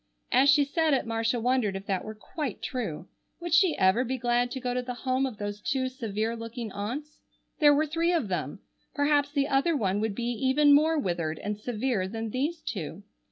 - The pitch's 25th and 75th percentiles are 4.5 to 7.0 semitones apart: Yes, average, 5.2 semitones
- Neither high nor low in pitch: No, high, 245 Hz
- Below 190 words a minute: No, fast, 205 wpm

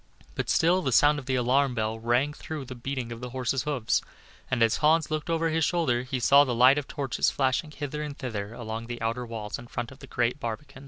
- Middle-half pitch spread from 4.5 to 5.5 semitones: No, average, 3.7 semitones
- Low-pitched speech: Yes, low, 130 Hz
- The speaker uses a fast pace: Yes, fast, 235 wpm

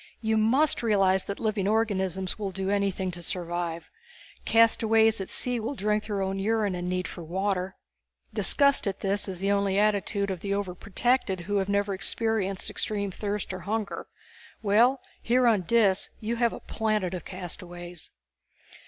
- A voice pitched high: Yes, high, 200 Hz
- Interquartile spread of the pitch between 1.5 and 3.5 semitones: Yes, average, 2.8 semitones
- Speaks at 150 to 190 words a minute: Yes, average, 165 wpm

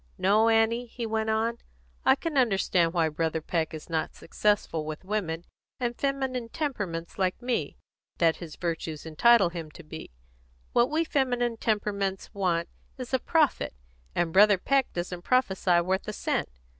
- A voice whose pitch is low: No, high, 200 Hz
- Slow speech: No, average, 160 wpm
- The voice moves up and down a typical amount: No, wide, 5.9 semitones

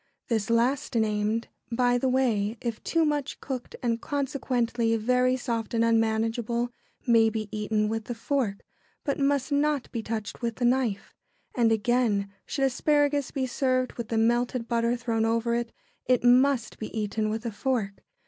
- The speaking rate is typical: Yes, average, 165 wpm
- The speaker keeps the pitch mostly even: Yes, narrow, 2.3 semitones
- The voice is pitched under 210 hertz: No, high, 235 Hz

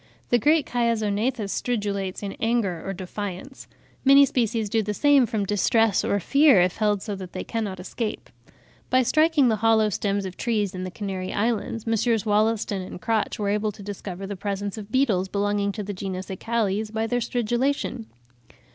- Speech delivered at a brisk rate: No, average, 175 wpm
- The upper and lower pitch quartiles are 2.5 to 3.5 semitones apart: Yes, average, 2.8 semitones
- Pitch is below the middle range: No, high, 210 Hz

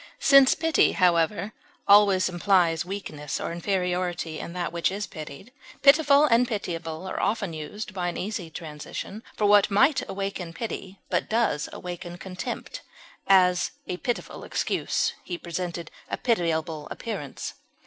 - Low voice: No, medium, 185 Hz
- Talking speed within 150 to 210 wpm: No, average, 140 wpm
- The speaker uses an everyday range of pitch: Yes, average, 3.5 semitones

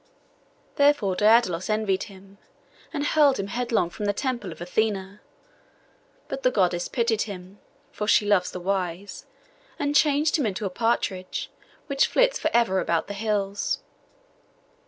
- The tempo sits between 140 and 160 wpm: Yes, average, 145 wpm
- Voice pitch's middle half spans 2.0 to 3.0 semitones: No, average, 4.2 semitones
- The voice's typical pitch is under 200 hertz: No, high, 205 Hz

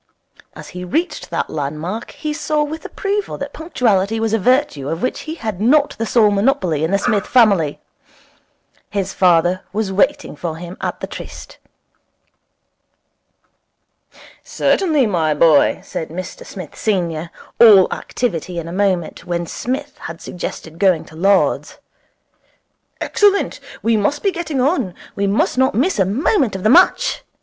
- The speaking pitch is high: Yes, high, 200 Hz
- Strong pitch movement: Yes, wide, 7.1 semitones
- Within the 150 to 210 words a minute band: Yes, average, 155 wpm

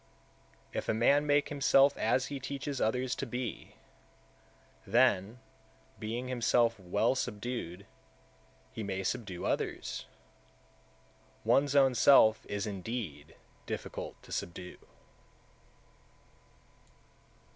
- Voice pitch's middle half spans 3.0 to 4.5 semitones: No, average, 5.0 semitones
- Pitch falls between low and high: No, low, 120 Hz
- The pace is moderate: No, slow, 100 wpm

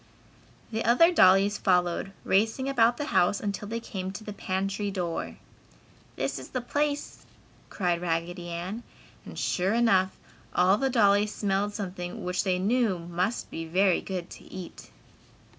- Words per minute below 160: Yes, average, 150 wpm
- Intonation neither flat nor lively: Yes, average, 3.7 semitones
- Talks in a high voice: Yes, high, 195 Hz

